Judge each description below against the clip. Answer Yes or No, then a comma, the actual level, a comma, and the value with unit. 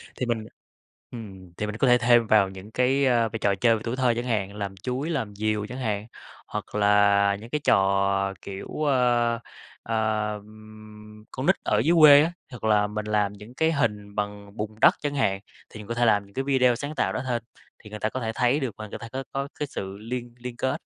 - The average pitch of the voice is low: Yes, low, 110 Hz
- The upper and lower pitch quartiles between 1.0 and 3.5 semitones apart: Yes, average, 3.2 semitones